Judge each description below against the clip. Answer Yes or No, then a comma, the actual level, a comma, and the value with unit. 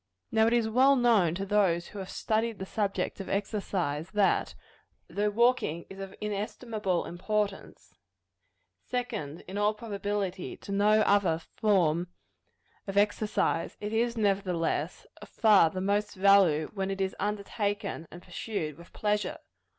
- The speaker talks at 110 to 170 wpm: Yes, average, 145 wpm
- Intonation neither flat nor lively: No, narrow, 2.3 semitones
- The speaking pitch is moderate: No, high, 200 Hz